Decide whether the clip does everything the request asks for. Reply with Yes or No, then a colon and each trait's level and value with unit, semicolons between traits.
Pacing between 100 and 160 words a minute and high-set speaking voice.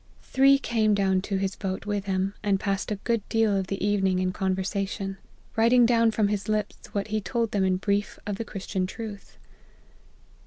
No: average, 185 wpm; high, 200 Hz